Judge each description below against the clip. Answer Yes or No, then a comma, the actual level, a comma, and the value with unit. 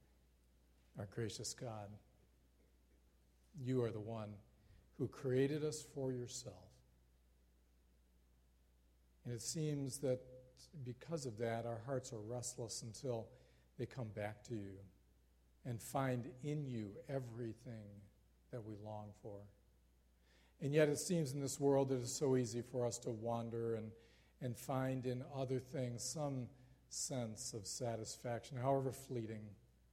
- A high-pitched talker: No, low, 115 Hz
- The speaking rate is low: Yes, slow, 130 wpm